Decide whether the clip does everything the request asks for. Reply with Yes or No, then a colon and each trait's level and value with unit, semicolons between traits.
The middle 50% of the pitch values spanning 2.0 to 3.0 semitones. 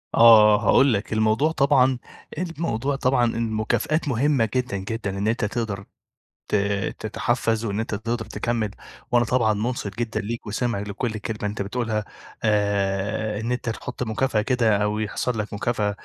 Yes: average, 2.7 semitones